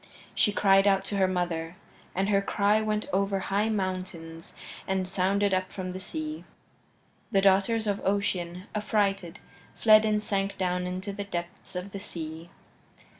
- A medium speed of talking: Yes, average, 155 wpm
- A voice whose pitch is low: No, high, 195 Hz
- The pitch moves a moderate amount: No, narrow, 2.0 semitones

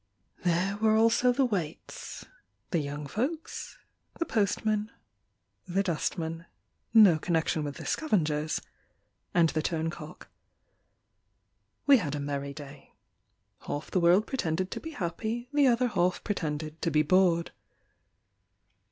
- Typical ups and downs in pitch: No, wide, 5.7 semitones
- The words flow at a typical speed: No, slow, 125 wpm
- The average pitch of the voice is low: No, medium, 175 Hz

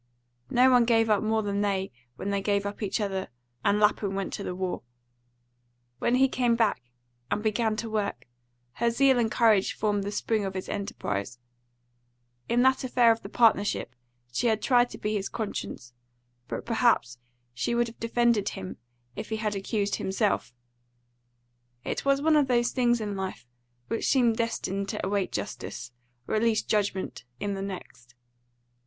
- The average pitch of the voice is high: Yes, high, 215 Hz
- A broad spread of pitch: No, average, 3.1 semitones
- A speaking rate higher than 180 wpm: No, average, 175 wpm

